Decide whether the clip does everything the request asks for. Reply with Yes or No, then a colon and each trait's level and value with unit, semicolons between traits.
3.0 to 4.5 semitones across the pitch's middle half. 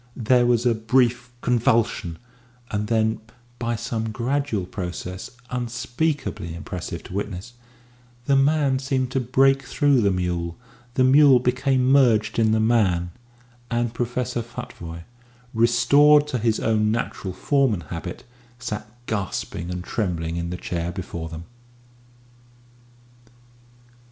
No: wide, 5.4 semitones